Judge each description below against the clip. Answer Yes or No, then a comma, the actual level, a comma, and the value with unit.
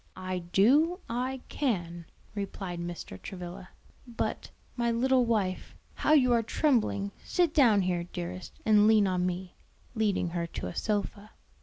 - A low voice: No, high, 200 Hz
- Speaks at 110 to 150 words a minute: Yes, average, 145 wpm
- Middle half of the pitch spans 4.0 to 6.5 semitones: Yes, average, 5.2 semitones